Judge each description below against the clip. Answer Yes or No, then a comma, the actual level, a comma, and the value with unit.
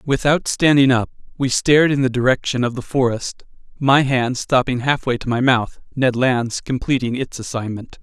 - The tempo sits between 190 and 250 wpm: No, average, 170 wpm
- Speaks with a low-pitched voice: Yes, low, 130 Hz